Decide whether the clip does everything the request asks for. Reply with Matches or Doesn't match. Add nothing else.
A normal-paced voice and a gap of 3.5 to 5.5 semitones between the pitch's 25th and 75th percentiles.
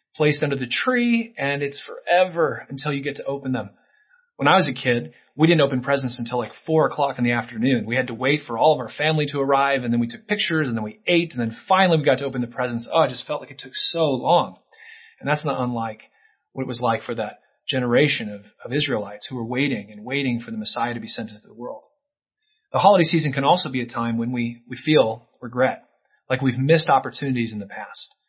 Doesn't match